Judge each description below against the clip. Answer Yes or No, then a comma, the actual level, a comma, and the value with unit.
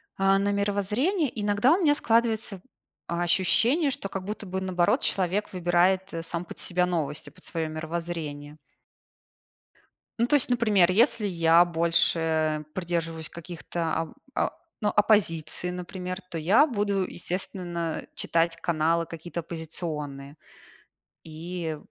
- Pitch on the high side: No, medium, 175 Hz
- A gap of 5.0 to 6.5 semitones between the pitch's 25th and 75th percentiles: No, average, 3.6 semitones